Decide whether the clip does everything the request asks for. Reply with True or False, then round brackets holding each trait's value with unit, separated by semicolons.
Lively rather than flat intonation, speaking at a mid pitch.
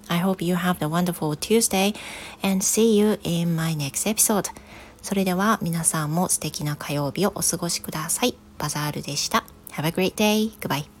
False (4.0 semitones; 175 Hz)